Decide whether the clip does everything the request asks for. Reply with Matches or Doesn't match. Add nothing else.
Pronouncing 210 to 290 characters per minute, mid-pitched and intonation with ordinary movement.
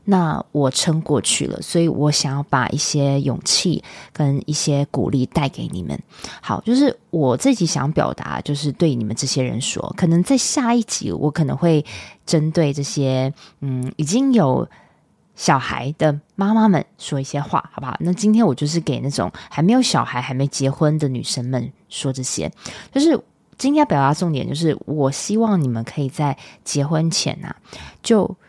Matches